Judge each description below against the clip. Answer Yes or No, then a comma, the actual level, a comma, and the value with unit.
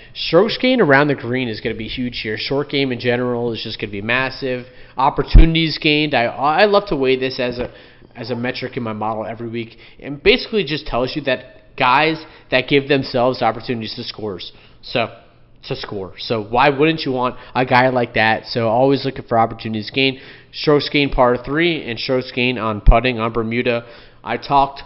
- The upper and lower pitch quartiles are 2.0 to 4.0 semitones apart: Yes, average, 2.8 semitones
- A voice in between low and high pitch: No, low, 125 Hz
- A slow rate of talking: No, average, 200 wpm